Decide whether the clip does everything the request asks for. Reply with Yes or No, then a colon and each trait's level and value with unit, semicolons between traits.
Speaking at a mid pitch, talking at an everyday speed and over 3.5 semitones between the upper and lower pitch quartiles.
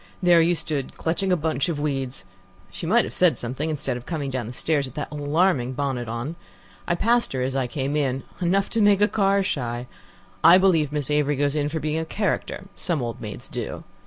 No: medium, 150 Hz; fast, 220 wpm; average, 4.5 semitones